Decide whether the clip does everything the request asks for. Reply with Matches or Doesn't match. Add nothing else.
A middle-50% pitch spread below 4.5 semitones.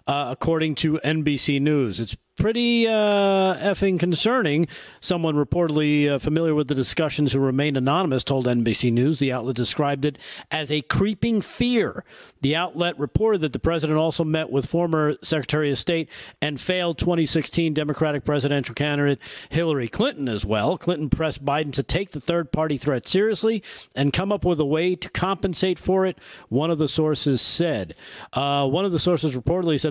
Matches